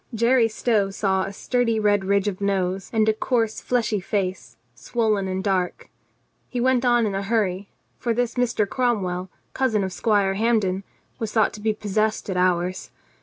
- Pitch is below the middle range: No, high, 210 Hz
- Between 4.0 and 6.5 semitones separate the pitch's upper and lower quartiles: No, average, 3.1 semitones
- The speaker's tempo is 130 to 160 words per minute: No, average, 170 wpm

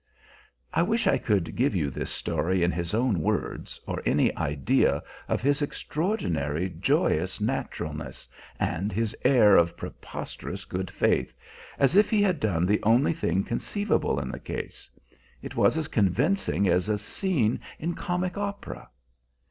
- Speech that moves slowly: No, average, 150 wpm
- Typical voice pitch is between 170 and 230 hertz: No, low, 110 Hz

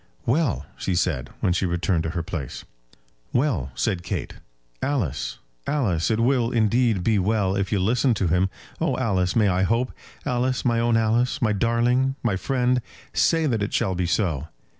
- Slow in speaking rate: No, average, 175 wpm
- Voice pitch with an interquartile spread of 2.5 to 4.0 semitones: No, average, 5.2 semitones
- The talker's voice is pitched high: No, low, 110 Hz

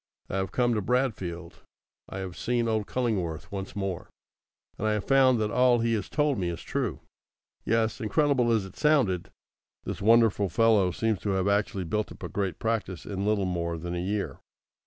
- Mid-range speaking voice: No, low, 105 Hz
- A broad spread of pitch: No, average, 3.5 semitones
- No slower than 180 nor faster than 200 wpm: Yes, average, 190 wpm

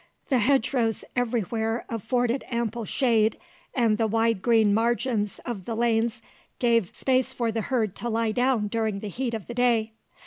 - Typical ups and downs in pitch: No, narrow, 1.7 semitones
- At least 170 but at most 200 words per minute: Yes, average, 175 wpm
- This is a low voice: No, high, 230 Hz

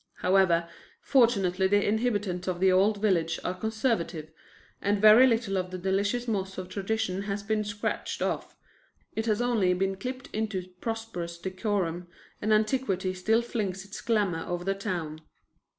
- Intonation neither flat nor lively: Yes, average, 3.1 semitones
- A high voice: Yes, high, 195 Hz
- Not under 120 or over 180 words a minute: Yes, average, 150 wpm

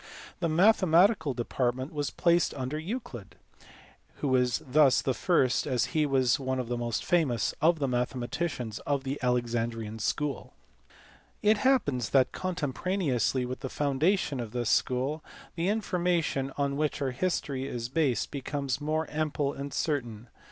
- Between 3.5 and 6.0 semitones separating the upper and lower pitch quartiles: Yes, average, 4.2 semitones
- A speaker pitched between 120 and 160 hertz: Yes, medium, 140 Hz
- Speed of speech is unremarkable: Yes, average, 150 wpm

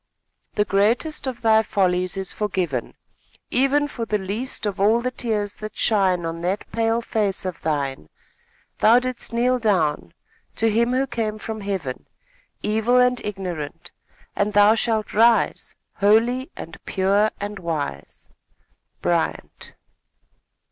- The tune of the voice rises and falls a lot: No, average, 3.6 semitones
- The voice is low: No, high, 210 Hz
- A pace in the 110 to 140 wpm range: Yes, slow, 135 wpm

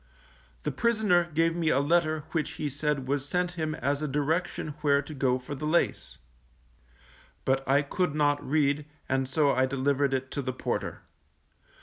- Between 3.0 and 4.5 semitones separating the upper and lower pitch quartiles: No, narrow, 2.5 semitones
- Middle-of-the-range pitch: Yes, medium, 145 Hz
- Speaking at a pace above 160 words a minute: Yes, average, 175 wpm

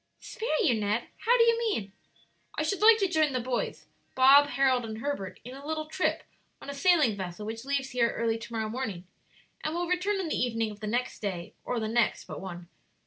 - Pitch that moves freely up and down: Yes, wide, 6.0 semitones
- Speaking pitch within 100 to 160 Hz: No, very high, 255 Hz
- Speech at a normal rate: No, fast, 220 wpm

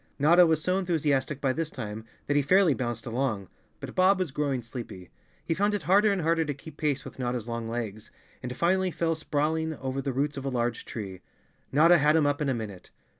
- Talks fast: Yes, fast, 220 wpm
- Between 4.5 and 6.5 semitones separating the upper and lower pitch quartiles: Yes, average, 5.1 semitones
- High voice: No, medium, 145 Hz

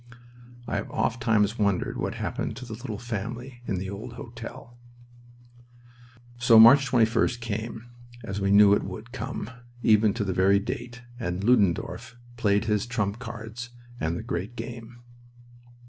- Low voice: Yes, low, 115 Hz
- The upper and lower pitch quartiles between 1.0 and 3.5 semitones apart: Yes, average, 2.9 semitones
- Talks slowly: No, average, 145 wpm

